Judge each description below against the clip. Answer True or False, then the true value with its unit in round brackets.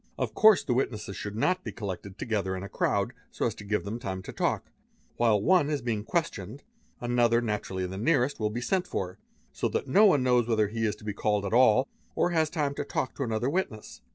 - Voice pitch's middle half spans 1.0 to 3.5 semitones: False (5.1 semitones)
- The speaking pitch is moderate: False (115 Hz)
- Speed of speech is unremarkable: False (230 wpm)